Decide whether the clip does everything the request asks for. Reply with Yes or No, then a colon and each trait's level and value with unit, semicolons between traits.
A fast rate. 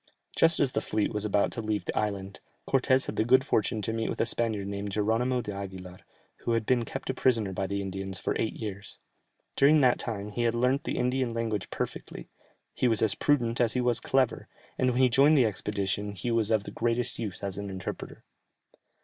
Yes: fast, 215 wpm